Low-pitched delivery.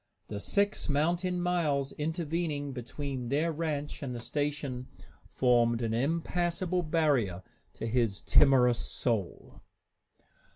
No: medium, 145 Hz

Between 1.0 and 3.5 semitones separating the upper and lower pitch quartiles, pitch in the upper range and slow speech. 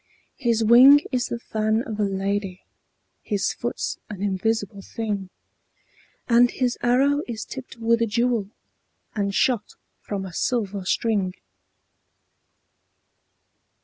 Yes: average, 3.1 semitones; high, 220 Hz; slow, 115 wpm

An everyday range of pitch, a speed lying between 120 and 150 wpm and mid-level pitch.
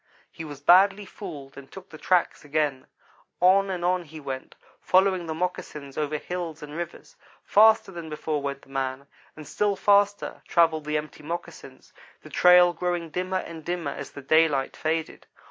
No: average, 3.4 semitones; average, 170 wpm; medium, 165 Hz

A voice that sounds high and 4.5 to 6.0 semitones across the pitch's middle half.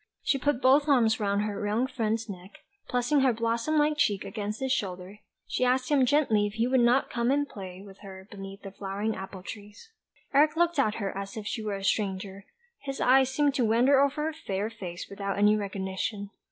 Yes: high, 220 Hz; average, 4.9 semitones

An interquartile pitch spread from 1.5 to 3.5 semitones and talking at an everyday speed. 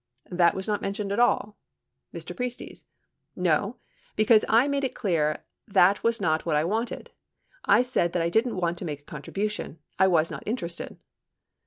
No: average, 5.1 semitones; average, 175 wpm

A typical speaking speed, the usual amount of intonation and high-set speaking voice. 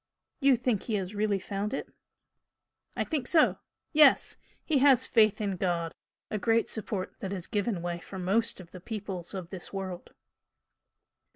Yes: average, 165 wpm; average, 3.8 semitones; high, 200 Hz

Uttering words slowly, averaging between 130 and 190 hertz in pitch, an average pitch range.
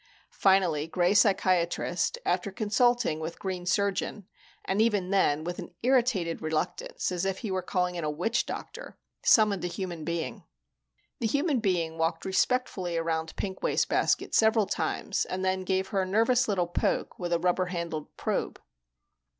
No: average, 160 wpm; medium, 185 Hz; average, 3.4 semitones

